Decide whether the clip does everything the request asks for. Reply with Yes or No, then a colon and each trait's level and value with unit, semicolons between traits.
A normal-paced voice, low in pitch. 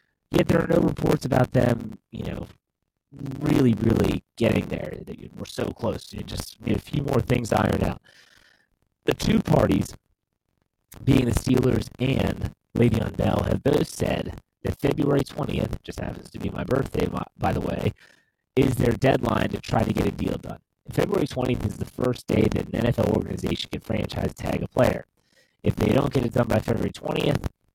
Yes: average, 175 wpm; low, 115 Hz